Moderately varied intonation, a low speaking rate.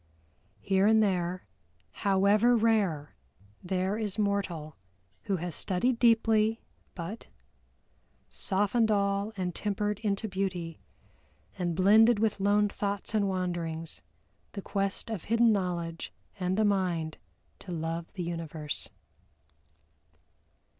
Yes: average, 3.2 semitones; slow, 110 wpm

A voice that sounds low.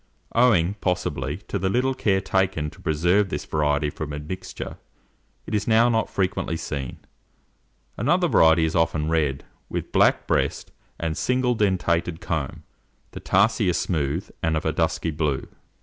Yes: very low, 85 Hz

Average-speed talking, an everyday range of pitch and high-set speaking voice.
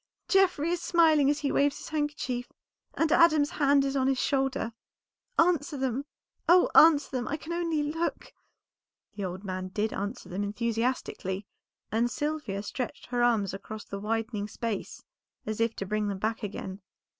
No: average, 165 wpm; wide, 6.0 semitones; very high, 250 Hz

